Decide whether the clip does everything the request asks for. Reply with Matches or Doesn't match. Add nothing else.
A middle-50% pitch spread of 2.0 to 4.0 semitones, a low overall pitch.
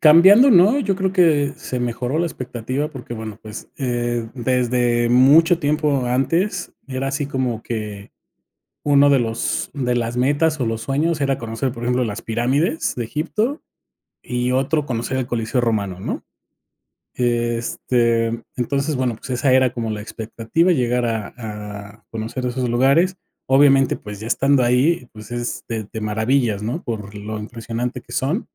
Matches